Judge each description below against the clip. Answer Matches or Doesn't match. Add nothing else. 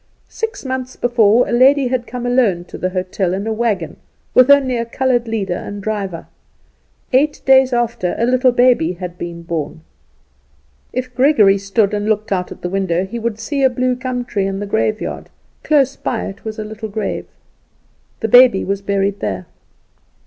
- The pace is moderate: Matches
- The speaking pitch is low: Doesn't match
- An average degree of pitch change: Matches